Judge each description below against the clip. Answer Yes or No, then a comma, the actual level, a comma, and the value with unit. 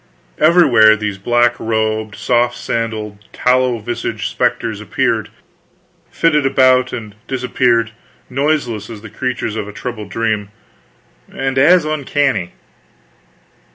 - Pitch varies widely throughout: No, average, 3.3 semitones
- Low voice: Yes, low, 120 Hz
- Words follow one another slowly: Yes, slow, 110 wpm